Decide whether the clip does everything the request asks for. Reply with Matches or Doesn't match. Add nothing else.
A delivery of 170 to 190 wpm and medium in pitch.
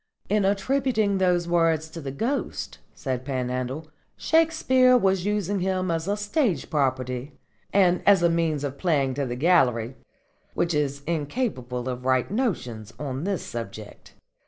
Doesn't match